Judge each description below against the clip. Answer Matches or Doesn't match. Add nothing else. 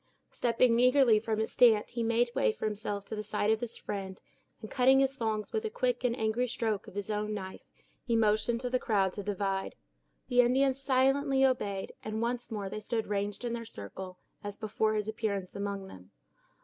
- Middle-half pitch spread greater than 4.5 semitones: Doesn't match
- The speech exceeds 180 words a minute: Matches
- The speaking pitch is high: Matches